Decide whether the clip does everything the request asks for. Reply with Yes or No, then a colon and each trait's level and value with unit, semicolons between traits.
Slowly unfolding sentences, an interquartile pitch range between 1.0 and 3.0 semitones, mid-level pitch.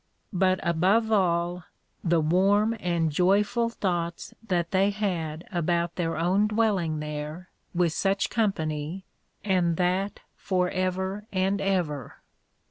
Yes: slow, 120 wpm; average, 2.7 semitones; medium, 180 Hz